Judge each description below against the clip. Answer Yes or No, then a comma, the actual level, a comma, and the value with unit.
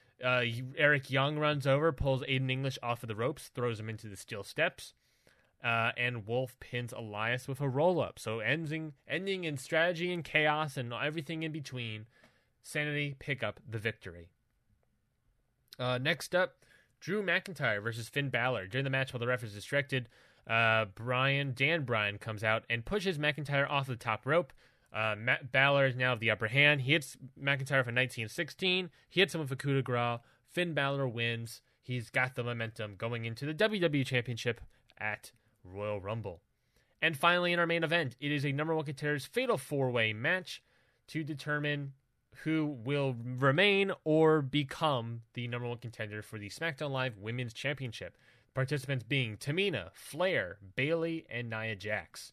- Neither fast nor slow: Yes, average, 170 wpm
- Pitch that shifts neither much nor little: Yes, average, 4.1 semitones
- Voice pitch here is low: Yes, low, 130 Hz